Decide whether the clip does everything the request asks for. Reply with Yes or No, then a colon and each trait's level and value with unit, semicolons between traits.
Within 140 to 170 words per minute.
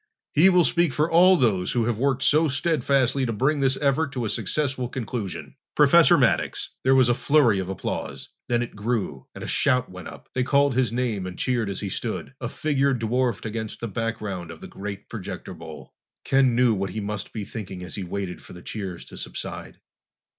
No: fast, 205 wpm